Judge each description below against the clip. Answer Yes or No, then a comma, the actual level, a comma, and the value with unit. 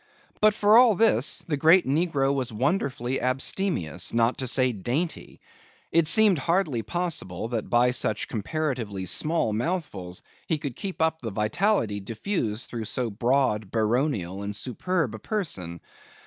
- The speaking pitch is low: Yes, low, 130 Hz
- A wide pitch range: Yes, wide, 7.4 semitones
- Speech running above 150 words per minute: No, average, 145 wpm